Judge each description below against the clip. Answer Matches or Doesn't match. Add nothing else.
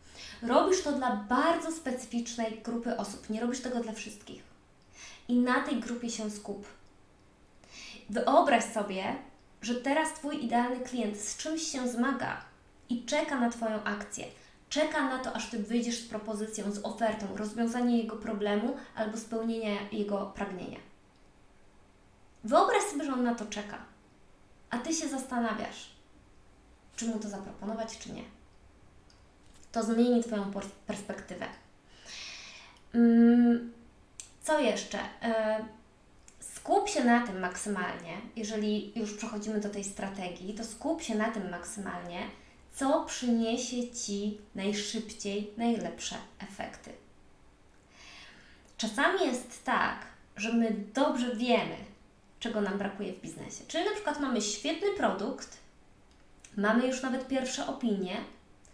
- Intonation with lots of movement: Doesn't match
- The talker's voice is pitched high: Matches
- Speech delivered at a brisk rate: Doesn't match